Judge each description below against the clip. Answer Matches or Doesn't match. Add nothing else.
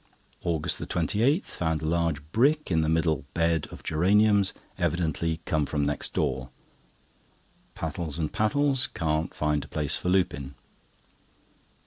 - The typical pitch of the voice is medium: Doesn't match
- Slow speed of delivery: Matches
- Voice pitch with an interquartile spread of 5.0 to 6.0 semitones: Doesn't match